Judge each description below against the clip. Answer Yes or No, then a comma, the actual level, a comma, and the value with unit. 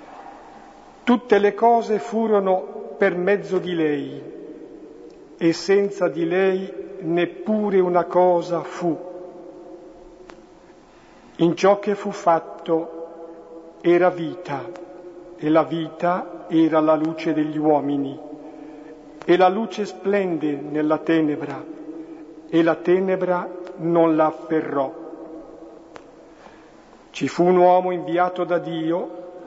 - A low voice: No, medium, 175 Hz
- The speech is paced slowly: Yes, slow, 100 wpm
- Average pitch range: No, narrow, 2.1 semitones